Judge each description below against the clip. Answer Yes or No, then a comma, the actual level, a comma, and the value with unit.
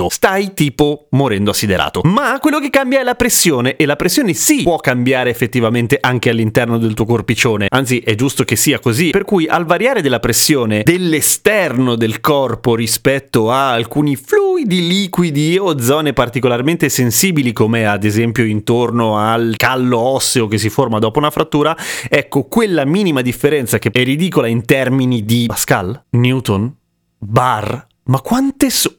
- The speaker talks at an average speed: Yes, average, 160 wpm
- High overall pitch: No, low, 130 Hz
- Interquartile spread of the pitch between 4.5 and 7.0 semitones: Yes, average, 5.2 semitones